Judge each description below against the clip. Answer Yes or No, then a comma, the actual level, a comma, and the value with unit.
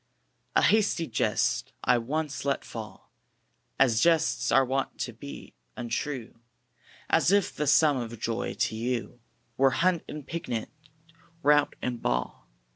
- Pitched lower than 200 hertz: Yes, low, 135 Hz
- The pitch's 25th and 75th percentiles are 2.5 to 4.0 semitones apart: No, average, 4.5 semitones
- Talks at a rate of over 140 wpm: No, slow, 135 wpm